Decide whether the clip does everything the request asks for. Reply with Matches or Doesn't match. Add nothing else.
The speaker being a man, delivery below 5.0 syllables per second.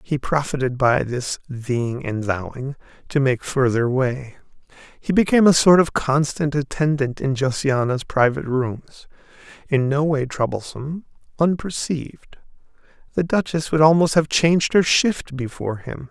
Matches